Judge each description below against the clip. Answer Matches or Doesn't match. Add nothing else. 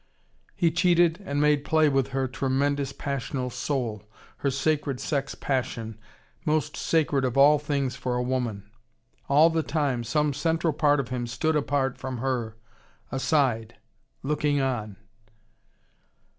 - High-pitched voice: Doesn't match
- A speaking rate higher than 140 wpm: Doesn't match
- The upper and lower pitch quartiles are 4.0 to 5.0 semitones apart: Doesn't match